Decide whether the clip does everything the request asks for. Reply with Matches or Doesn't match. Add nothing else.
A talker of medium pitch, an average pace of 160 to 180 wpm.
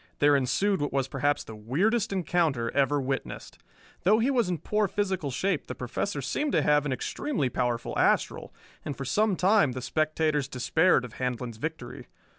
Matches